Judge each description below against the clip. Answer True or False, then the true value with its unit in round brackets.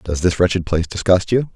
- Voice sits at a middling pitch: False (90 Hz)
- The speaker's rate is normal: False (230 wpm)